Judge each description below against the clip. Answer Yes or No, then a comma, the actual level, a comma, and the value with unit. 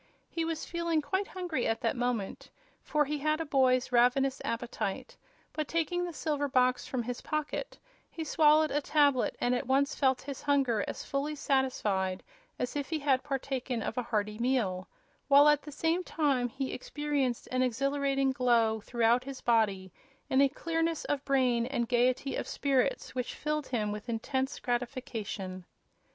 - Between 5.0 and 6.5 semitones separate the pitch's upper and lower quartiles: No, average, 3.4 semitones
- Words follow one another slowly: No, average, 170 wpm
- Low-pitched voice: No, very high, 265 Hz